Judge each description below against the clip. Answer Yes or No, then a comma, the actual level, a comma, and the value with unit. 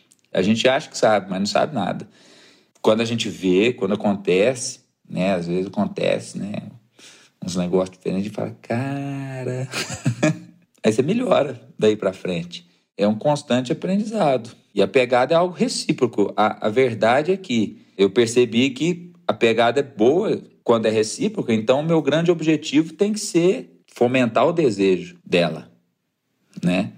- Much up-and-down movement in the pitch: Yes, wide, 7.1 semitones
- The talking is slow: No, average, 155 wpm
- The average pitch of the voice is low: Yes, low, 120 Hz